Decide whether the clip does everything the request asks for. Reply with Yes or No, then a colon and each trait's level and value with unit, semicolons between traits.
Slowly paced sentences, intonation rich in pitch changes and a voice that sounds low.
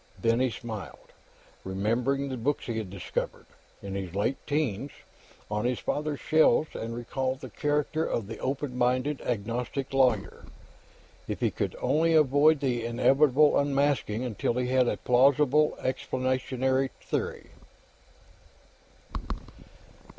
No: slow, 120 wpm; average, 3.4 semitones; low, 130 Hz